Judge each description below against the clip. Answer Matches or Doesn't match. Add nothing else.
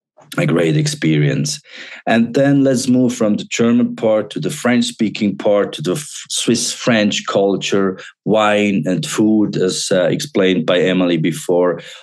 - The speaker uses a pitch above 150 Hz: Doesn't match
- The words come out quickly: Doesn't match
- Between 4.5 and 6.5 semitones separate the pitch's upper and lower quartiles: Matches